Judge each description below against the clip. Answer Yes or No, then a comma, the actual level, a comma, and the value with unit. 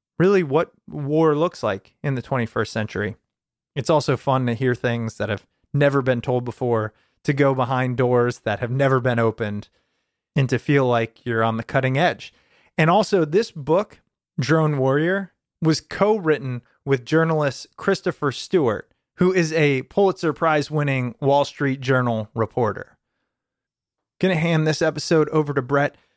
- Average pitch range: Yes, average, 4.5 semitones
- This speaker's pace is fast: No, average, 160 wpm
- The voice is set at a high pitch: No, medium, 140 Hz